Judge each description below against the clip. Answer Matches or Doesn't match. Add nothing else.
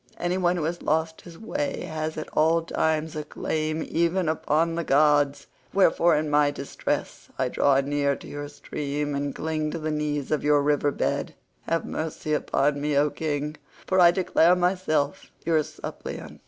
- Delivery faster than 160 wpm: Matches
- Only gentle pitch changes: Matches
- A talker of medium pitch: Matches